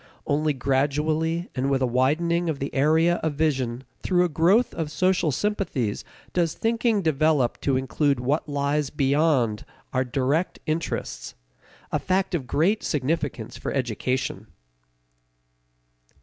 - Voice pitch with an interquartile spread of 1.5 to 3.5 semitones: No, average, 4.0 semitones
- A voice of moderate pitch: Yes, medium, 150 Hz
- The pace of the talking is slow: Yes, slow, 130 wpm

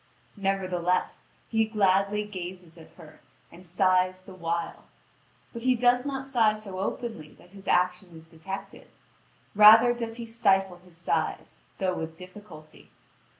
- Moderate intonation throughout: Yes, average, 3.5 semitones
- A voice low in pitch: No, high, 190 Hz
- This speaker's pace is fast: No, average, 140 wpm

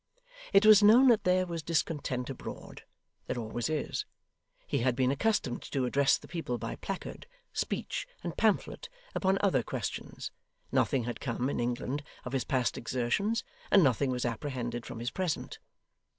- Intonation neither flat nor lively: No, wide, 6.9 semitones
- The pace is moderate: Yes, average, 160 wpm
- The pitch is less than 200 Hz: Yes, low, 135 Hz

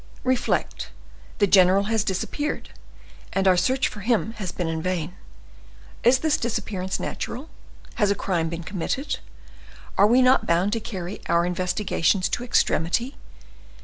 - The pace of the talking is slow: No, average, 145 wpm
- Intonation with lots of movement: No, average, 4.8 semitones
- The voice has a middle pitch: No, high, 200 Hz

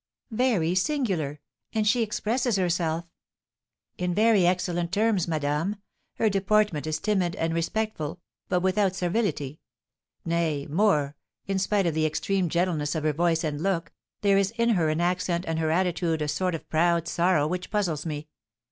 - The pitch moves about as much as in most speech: Yes, average, 3.7 semitones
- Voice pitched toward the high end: No, medium, 175 Hz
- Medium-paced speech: Yes, average, 160 wpm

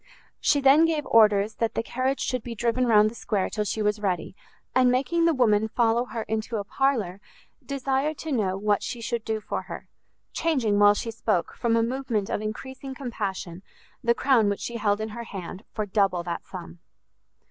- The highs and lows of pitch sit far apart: No, average, 3.6 semitones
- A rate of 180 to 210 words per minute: Yes, average, 195 wpm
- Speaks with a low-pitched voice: No, high, 225 Hz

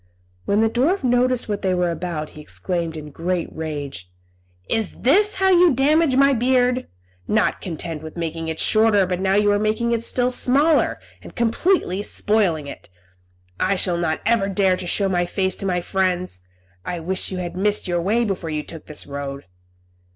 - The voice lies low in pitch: No, high, 190 Hz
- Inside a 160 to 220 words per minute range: Yes, average, 190 wpm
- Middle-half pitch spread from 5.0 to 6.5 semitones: Yes, wide, 5.6 semitones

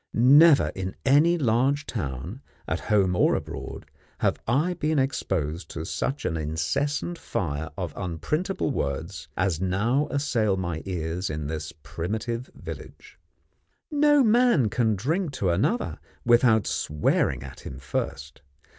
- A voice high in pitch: No, low, 105 Hz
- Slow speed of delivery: Yes, slow, 130 wpm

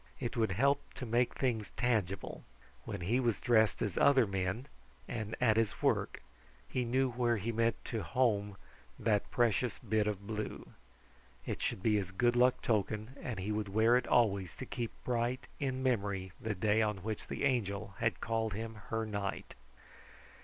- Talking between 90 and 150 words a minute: No, average, 175 wpm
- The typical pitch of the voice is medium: No, low, 110 Hz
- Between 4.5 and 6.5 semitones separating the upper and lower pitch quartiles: No, average, 3.0 semitones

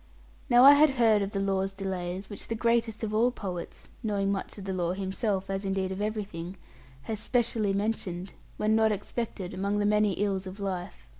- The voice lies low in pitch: No, high, 200 Hz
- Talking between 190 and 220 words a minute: Yes, average, 200 wpm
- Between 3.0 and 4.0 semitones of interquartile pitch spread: No, narrow, 2.4 semitones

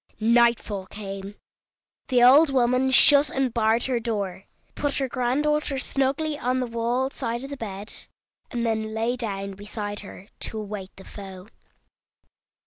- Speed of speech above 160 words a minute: No, average, 145 wpm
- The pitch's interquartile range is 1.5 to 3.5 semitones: No, average, 4.2 semitones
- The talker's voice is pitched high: Yes, high, 235 Hz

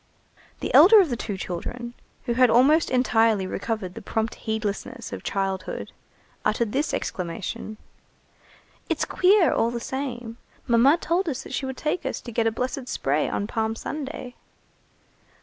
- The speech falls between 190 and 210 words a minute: No, average, 155 wpm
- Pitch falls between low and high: No, high, 235 Hz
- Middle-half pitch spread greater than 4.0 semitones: No, average, 3.5 semitones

